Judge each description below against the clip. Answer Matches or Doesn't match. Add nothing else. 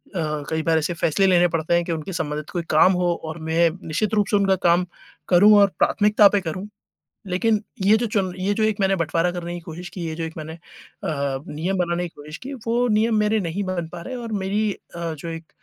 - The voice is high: Doesn't match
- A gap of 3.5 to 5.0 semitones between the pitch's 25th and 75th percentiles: Matches